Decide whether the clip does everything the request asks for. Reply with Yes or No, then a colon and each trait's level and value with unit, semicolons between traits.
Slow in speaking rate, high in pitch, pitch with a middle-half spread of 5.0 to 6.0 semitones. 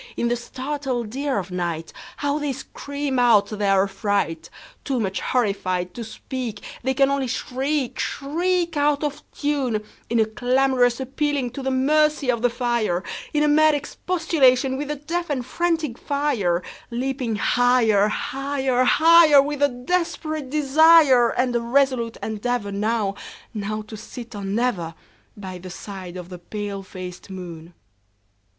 Yes: slow, 125 wpm; very high, 250 Hz; wide, 5.5 semitones